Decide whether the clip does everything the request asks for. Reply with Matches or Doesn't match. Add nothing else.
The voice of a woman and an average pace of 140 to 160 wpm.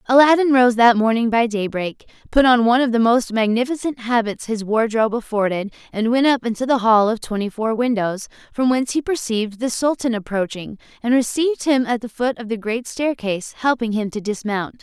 Doesn't match